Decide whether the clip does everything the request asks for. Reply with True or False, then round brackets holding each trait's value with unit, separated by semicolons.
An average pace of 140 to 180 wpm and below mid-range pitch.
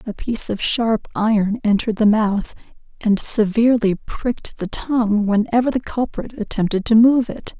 False (160 wpm; 220 Hz)